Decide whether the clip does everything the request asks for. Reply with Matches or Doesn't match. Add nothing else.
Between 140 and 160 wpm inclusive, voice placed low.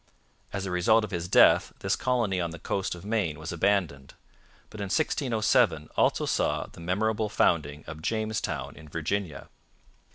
Matches